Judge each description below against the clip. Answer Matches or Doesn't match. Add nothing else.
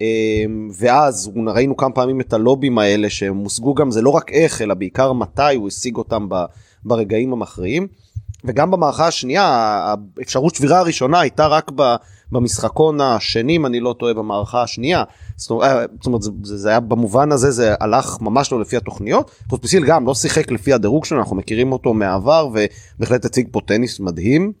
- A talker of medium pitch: Doesn't match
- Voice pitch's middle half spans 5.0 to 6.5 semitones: Doesn't match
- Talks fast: Matches